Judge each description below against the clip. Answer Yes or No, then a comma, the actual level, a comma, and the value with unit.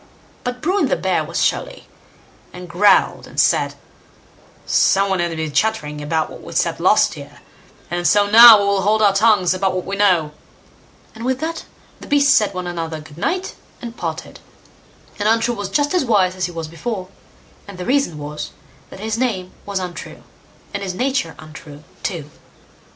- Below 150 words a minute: No, average, 180 wpm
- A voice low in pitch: No, high, 195 Hz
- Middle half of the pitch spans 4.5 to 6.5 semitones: Yes, average, 4.8 semitones